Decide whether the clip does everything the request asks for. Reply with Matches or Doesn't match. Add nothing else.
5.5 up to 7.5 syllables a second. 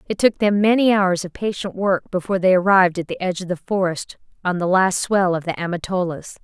Matches